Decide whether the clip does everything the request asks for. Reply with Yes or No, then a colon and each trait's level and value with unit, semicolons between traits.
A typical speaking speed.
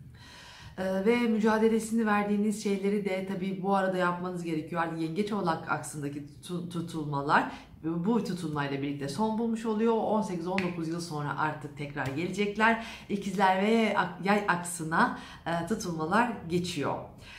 Yes: average, 115 wpm